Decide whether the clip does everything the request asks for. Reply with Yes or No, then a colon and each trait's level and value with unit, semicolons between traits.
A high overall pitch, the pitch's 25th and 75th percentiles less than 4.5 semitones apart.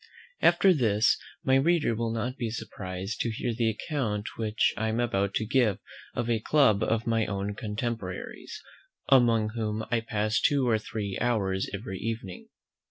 No: low, 110 Hz; narrow, 2.4 semitones